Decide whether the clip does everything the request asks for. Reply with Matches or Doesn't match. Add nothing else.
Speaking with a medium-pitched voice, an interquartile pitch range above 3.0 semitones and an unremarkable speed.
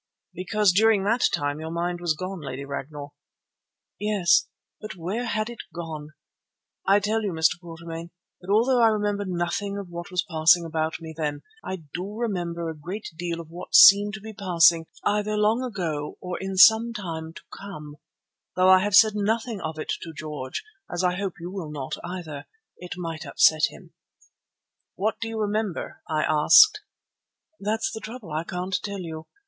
Matches